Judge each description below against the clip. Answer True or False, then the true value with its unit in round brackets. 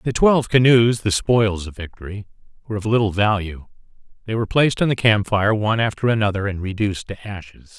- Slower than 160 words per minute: False (195 wpm)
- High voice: False (105 Hz)